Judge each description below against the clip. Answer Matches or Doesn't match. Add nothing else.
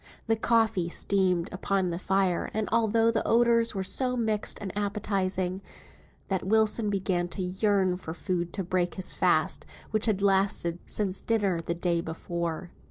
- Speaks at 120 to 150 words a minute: Doesn't match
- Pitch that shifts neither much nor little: Matches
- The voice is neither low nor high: Doesn't match